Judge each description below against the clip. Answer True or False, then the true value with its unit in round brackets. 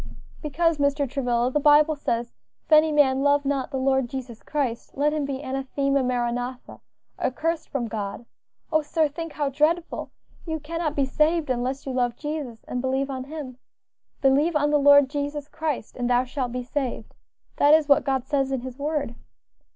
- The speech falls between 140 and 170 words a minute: False (180 wpm)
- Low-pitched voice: False (275 Hz)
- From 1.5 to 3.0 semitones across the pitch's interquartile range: True (2.7 semitones)